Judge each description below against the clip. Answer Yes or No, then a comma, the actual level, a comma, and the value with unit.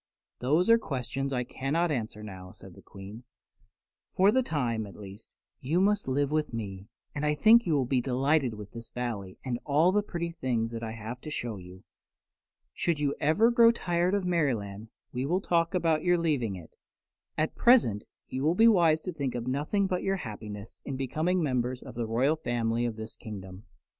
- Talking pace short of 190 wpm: No, average, 195 wpm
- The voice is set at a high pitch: No, low, 135 Hz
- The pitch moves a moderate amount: No, wide, 6.9 semitones